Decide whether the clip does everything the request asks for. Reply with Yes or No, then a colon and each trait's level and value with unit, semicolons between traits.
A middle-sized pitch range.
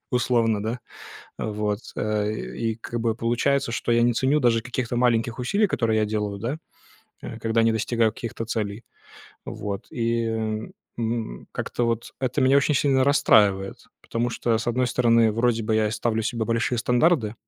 No: narrow, 1.9 semitones